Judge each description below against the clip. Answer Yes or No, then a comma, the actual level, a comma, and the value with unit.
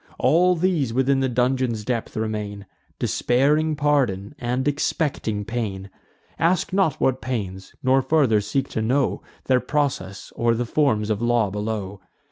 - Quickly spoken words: No, average, 140 wpm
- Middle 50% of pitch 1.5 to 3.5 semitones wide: No, average, 4.9 semitones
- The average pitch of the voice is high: No, low, 125 Hz